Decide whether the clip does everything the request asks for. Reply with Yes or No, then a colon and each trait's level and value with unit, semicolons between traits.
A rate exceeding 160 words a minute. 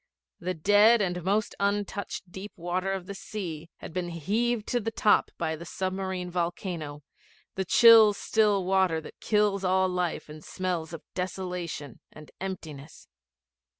No: average, 150 wpm